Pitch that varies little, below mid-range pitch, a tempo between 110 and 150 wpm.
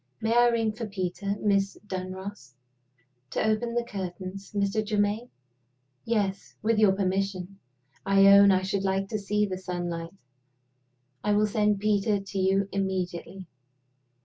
No: narrow, 1.8 semitones; high, 200 Hz; average, 140 wpm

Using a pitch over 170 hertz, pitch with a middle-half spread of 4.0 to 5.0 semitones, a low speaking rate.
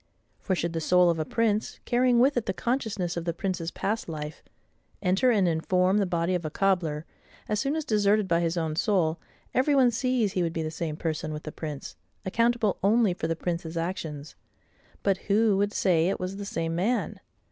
No: medium, 185 Hz; average, 4.5 semitones; fast, 205 wpm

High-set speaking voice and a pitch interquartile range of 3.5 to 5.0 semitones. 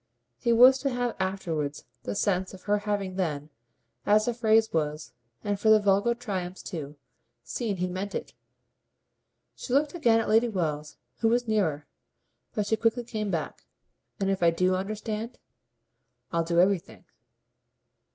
Yes: high, 200 Hz; average, 4.1 semitones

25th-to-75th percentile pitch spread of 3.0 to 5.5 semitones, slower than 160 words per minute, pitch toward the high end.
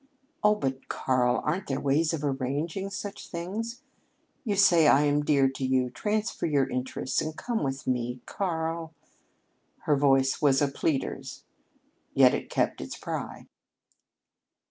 No: average, 4.8 semitones; average, 145 wpm; medium, 145 Hz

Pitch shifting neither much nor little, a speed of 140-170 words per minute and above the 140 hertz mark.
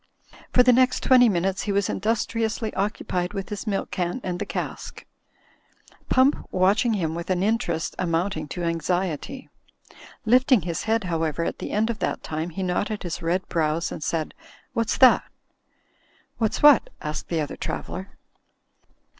Yes: average, 4.9 semitones; average, 165 wpm; high, 190 Hz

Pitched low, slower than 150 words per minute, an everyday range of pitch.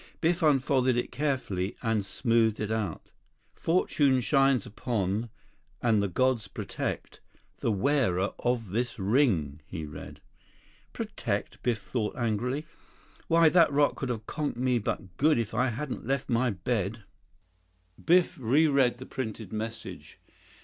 Yes: low, 120 Hz; slow, 135 wpm; average, 4.2 semitones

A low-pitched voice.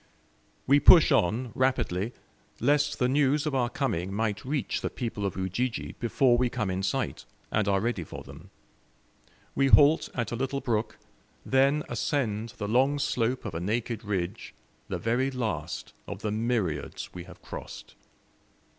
Yes: low, 120 Hz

